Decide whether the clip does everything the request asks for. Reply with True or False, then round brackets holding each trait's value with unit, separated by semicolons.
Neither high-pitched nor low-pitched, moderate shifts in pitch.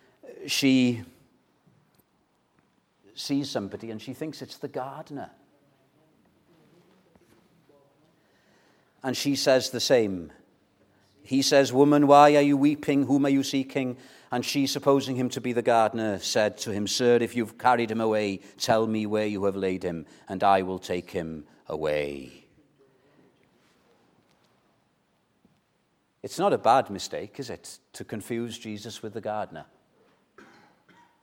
False (120 Hz; 4.8 semitones)